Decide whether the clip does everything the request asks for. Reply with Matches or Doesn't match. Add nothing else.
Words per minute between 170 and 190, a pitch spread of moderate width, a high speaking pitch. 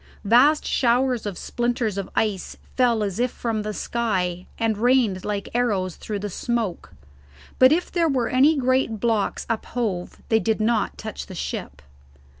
Doesn't match